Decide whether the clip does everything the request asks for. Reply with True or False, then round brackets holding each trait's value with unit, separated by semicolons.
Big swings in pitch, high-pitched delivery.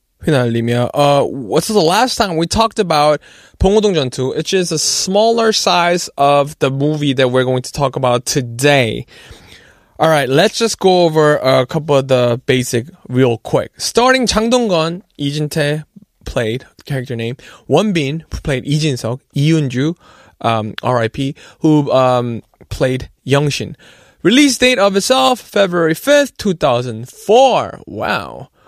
False (6.6 semitones; 150 Hz)